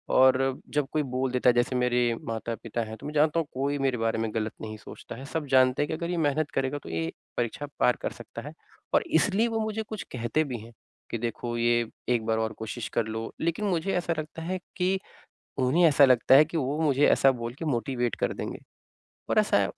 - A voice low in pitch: Yes, low, 130 Hz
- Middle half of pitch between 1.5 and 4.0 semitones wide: No, average, 4.8 semitones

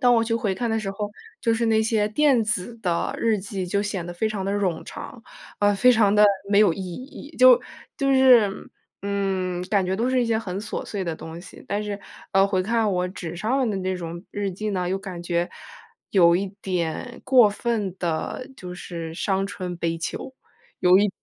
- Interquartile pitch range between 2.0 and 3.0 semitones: No, average, 3.7 semitones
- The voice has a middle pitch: No, high, 200 Hz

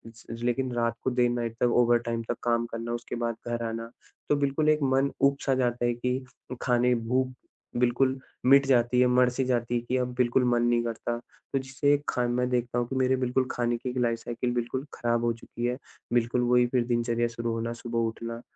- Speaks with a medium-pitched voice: No, low, 120 Hz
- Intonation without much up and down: Yes, narrow, 1.3 semitones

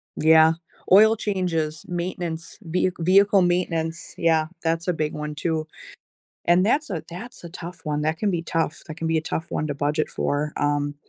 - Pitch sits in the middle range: Yes, medium, 165 Hz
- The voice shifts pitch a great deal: No, narrow, 2.5 semitones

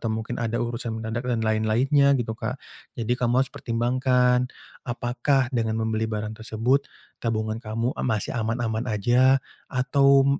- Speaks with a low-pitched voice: Yes, low, 115 Hz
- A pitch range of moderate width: No, narrow, 2.0 semitones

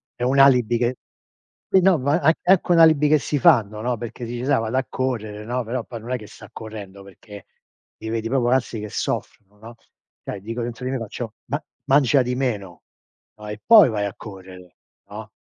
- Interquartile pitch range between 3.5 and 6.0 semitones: Yes, average, 3.8 semitones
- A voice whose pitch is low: Yes, low, 120 Hz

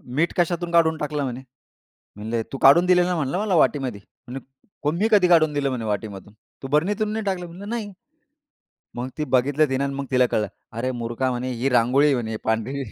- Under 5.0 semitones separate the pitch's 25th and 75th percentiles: No, wide, 5.6 semitones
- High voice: No, medium, 140 Hz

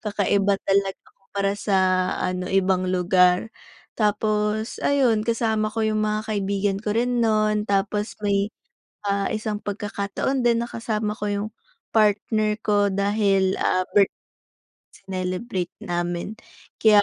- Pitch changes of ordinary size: No, narrow, 1.7 semitones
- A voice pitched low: No, high, 205 Hz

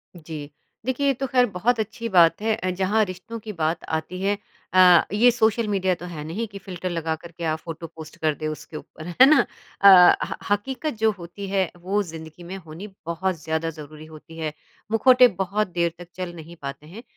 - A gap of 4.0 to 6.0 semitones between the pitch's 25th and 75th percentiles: Yes, average, 4.5 semitones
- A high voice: No, medium, 180 Hz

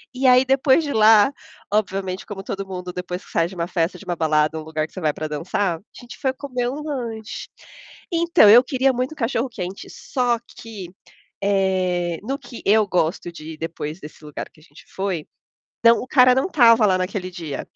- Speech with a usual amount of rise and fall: No, wide, 6.1 semitones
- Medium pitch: No, high, 195 Hz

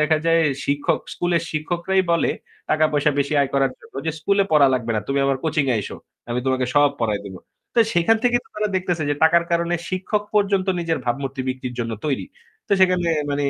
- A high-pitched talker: No, medium, 155 Hz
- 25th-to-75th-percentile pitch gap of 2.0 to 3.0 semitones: No, average, 4.3 semitones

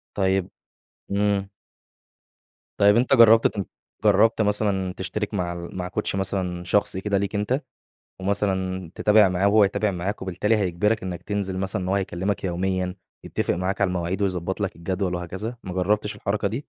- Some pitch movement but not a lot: No, narrow, 2.0 semitones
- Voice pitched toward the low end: Yes, very low, 95 Hz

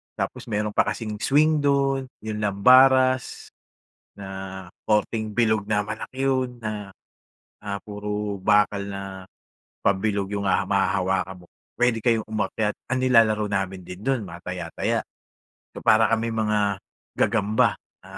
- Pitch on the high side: No, low, 105 Hz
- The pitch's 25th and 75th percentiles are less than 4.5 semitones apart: Yes, narrow, 2.6 semitones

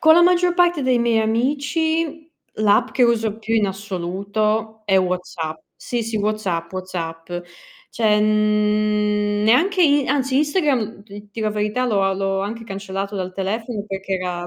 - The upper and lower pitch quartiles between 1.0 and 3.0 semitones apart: No, average, 4.0 semitones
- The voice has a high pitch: Yes, high, 215 Hz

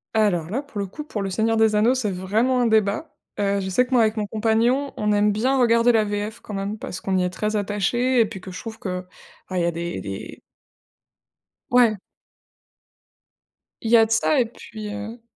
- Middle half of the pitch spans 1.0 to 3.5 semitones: Yes, average, 2.8 semitones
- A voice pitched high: Yes, high, 215 Hz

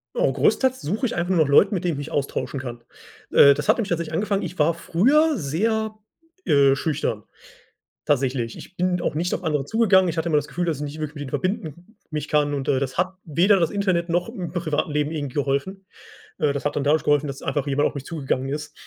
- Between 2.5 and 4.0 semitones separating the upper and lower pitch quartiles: No, average, 4.4 semitones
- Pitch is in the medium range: Yes, medium, 155 Hz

